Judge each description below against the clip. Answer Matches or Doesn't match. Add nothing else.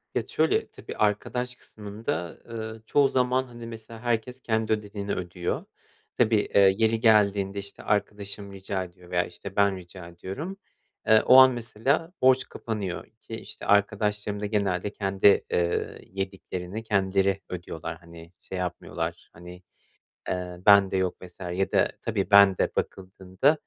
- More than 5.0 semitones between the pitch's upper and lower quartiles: Doesn't match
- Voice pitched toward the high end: Doesn't match